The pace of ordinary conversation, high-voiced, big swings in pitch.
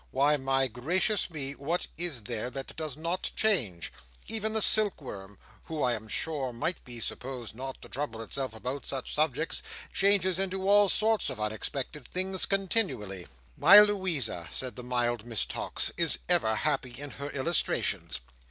No: average, 160 wpm; medium, 140 Hz; wide, 7.1 semitones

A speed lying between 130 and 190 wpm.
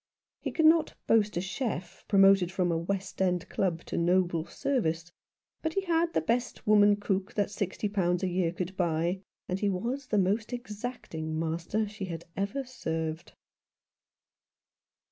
Yes: average, 160 wpm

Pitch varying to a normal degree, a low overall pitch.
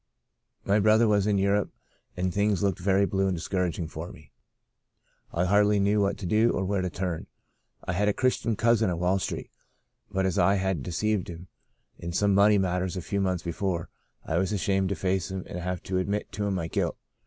No: narrow, 2.2 semitones; very low, 95 Hz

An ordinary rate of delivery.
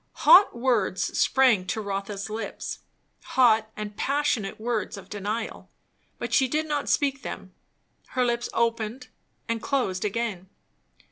No: slow, 130 wpm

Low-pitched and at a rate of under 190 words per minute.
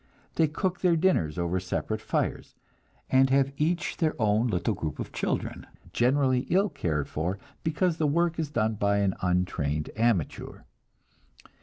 Yes: low, 120 Hz; average, 150 wpm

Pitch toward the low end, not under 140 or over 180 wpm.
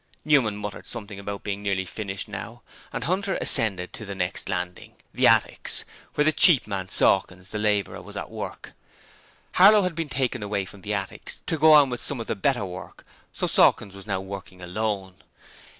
No: low, 105 Hz; average, 190 wpm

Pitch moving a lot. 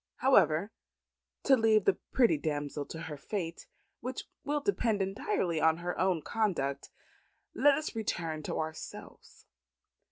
Yes: wide, 6.1 semitones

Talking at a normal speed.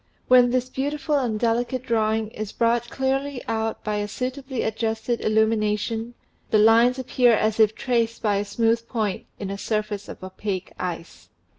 Yes: average, 160 wpm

